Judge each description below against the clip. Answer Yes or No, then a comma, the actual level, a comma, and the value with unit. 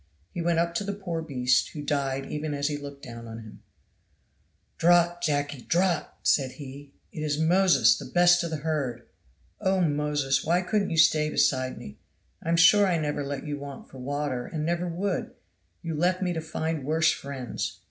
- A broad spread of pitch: No, average, 3.5 semitones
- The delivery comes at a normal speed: Yes, average, 190 wpm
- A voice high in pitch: No, medium, 155 Hz